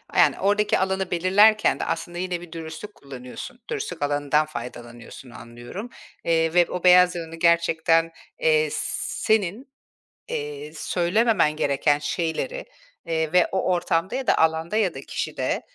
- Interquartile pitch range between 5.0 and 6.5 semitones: No, average, 4.5 semitones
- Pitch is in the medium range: Yes, medium, 175 Hz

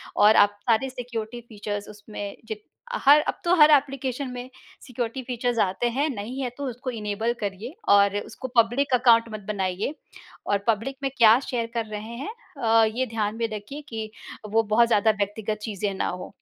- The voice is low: No, high, 225 Hz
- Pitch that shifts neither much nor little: Yes, average, 3.1 semitones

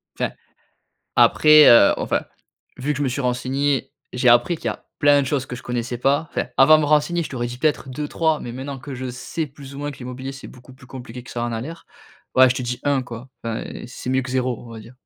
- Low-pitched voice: Yes, low, 130 Hz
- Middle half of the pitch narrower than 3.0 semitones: Yes, narrow, 2.6 semitones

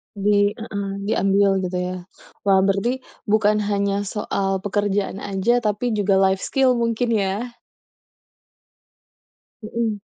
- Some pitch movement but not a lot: No, narrow, 2.0 semitones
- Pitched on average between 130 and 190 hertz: No, high, 205 Hz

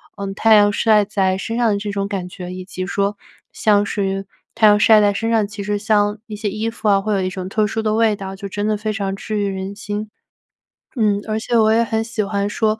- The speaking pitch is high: Yes, high, 205 Hz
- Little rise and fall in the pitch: Yes, narrow, 1.5 semitones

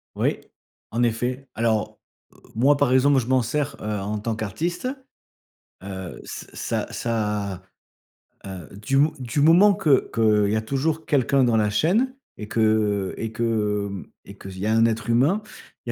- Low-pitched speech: Yes, low, 115 Hz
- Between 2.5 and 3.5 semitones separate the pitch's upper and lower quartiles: No, average, 4.6 semitones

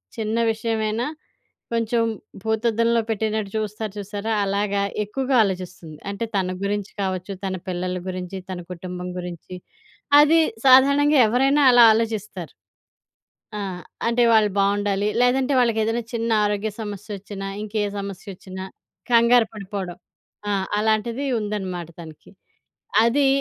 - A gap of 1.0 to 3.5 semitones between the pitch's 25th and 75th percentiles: Yes, average, 3.1 semitones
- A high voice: Yes, high, 210 Hz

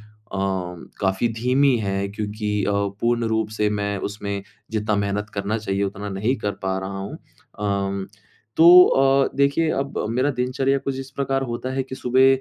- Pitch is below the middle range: Yes, low, 110 Hz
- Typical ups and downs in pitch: Yes, average, 4.7 semitones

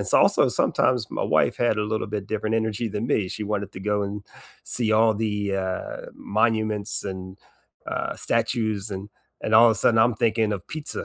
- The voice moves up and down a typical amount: No, narrow, 1.8 semitones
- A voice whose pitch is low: Yes, low, 110 Hz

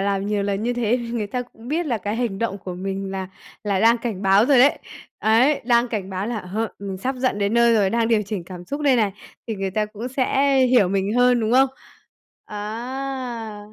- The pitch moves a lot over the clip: No, average, 3.7 semitones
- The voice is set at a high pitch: Yes, high, 220 Hz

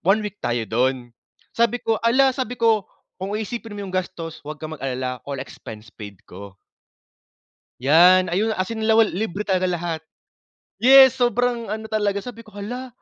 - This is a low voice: No, high, 200 Hz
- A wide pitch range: Yes, wide, 6.7 semitones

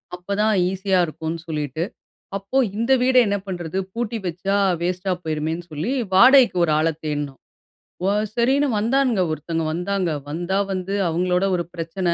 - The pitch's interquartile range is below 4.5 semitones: Yes, average, 3.8 semitones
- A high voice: No, medium, 180 Hz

